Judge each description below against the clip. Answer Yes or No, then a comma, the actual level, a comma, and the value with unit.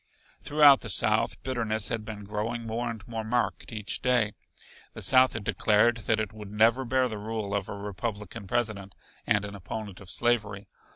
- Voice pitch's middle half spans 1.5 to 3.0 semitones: Yes, narrow, 2.5 semitones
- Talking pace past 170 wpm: Yes, average, 180 wpm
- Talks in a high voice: No, low, 110 Hz